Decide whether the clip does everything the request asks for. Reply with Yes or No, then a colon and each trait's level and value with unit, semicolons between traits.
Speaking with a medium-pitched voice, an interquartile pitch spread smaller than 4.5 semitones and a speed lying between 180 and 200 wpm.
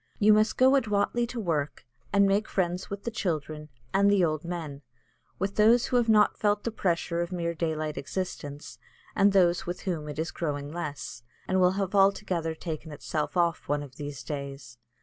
No: medium, 175 Hz; average, 4.8 semitones; average, 190 wpm